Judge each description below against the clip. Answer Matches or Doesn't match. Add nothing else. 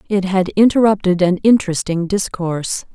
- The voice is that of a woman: Matches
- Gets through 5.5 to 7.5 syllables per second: Doesn't match